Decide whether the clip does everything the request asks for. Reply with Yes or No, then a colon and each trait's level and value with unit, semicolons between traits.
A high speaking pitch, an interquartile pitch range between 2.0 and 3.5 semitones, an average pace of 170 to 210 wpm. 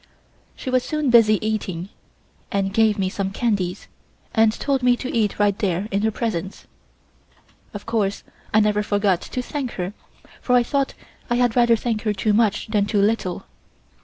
Yes: high, 215 Hz; average, 3.0 semitones; average, 175 wpm